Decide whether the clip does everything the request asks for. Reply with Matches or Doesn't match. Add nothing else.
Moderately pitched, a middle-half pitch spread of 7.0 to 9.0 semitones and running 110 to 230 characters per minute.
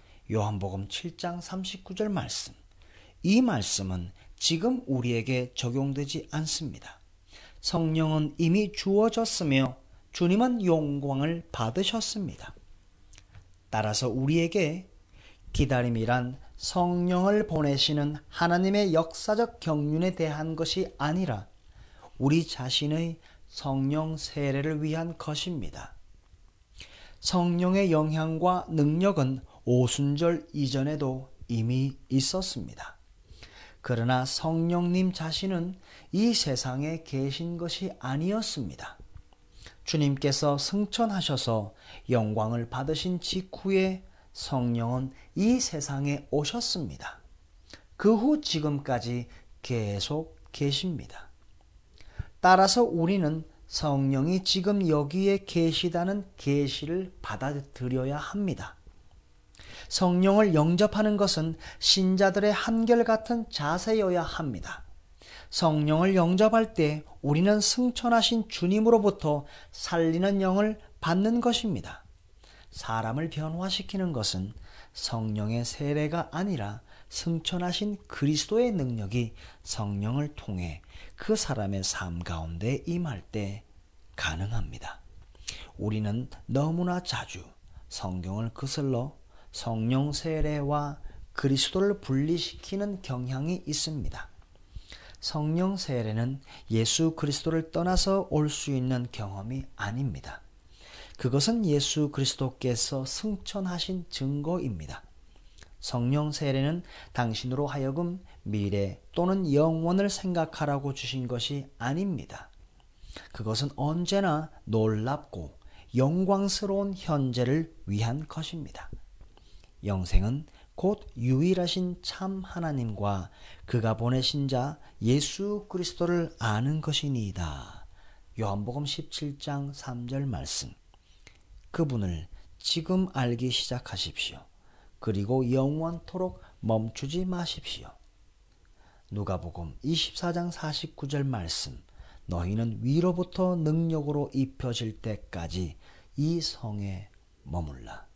Matches